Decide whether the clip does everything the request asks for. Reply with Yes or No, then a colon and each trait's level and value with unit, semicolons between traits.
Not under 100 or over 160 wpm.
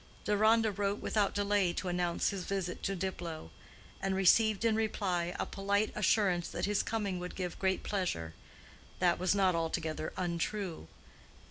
Yes: average, 150 wpm